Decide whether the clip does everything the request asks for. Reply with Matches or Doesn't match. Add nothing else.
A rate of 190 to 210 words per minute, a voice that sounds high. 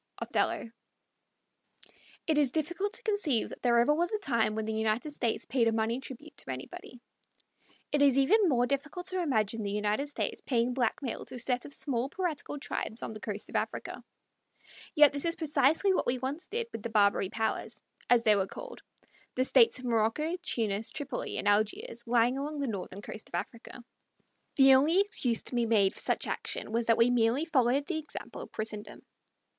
Matches